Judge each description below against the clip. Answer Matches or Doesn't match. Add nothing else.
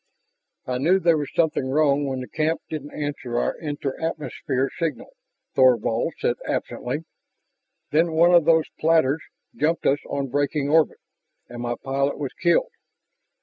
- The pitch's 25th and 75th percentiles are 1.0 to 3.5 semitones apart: Matches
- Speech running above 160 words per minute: Doesn't match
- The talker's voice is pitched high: Doesn't match